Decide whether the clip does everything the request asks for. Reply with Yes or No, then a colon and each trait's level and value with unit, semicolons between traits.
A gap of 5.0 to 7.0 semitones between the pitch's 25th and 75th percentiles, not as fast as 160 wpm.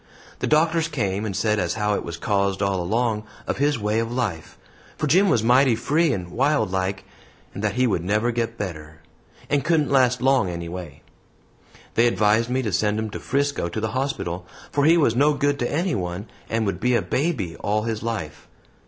No: wide, 5.6 semitones; average, 200 wpm